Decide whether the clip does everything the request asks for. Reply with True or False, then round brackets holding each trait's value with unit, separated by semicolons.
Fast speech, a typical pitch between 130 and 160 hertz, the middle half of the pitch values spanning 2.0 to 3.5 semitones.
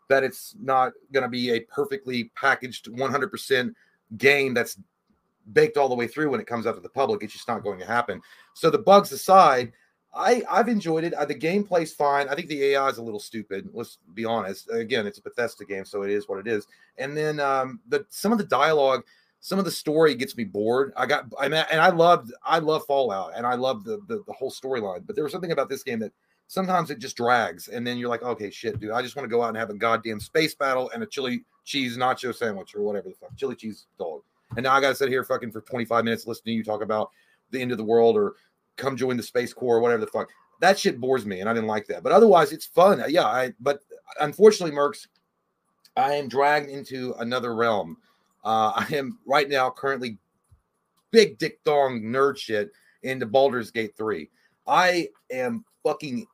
False (230 wpm; 135 Hz; 5.4 semitones)